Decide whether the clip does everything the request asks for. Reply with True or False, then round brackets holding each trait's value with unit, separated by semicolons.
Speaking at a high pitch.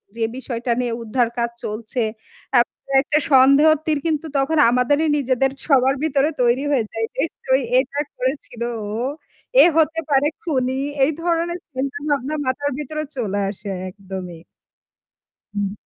True (265 Hz)